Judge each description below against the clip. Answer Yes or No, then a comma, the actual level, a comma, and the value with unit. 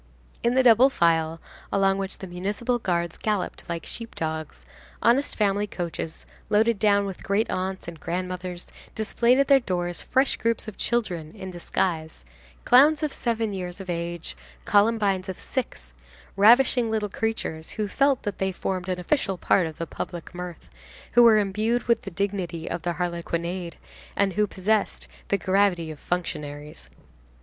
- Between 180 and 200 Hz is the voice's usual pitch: Yes, high, 190 Hz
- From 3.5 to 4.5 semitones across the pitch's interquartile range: Yes, average, 4.2 semitones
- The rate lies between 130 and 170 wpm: Yes, average, 160 wpm